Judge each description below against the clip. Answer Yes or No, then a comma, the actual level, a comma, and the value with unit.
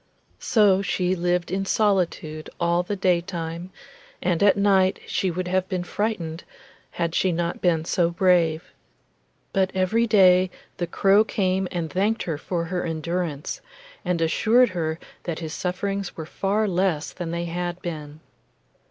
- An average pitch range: No, narrow, 2.3 semitones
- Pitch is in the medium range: Yes, medium, 180 Hz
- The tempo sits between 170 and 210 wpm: No, average, 150 wpm